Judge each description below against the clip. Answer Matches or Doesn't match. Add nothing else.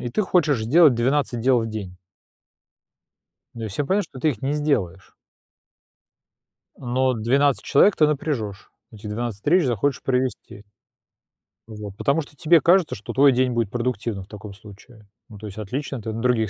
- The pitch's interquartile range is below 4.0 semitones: Doesn't match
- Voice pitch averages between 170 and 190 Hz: Doesn't match